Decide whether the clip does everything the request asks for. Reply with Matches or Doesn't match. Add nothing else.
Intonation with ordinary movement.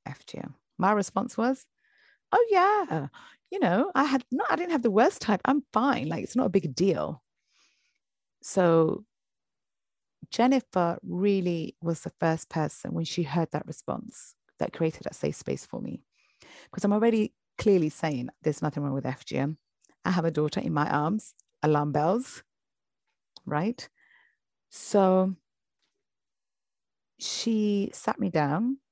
Doesn't match